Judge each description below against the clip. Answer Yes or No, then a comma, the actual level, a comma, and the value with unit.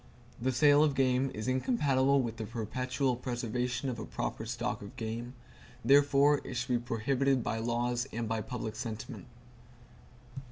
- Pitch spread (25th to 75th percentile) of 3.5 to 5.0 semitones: No, average, 2.7 semitones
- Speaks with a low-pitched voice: Yes, low, 125 Hz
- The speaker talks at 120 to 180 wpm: Yes, average, 155 wpm